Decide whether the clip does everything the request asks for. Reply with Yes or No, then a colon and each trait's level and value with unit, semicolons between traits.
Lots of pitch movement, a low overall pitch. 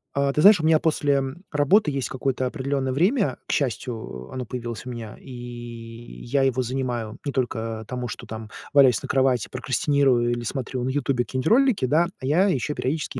No: average, 3.1 semitones; low, 130 Hz